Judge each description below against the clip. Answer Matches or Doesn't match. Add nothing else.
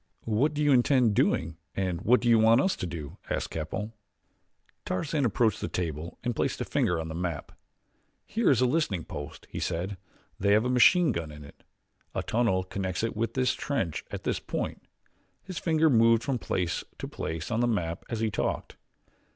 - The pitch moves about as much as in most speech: Doesn't match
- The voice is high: Doesn't match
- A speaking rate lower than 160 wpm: Doesn't match